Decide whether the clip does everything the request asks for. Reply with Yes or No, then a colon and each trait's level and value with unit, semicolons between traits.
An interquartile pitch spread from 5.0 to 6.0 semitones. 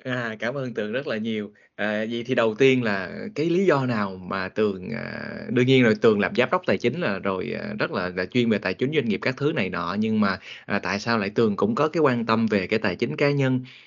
No: average, 4.0 semitones